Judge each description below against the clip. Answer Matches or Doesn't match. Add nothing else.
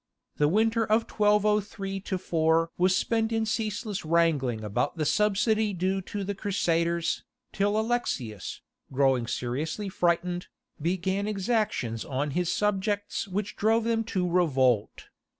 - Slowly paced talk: Matches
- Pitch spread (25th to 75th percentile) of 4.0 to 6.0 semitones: Matches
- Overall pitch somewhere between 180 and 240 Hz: Matches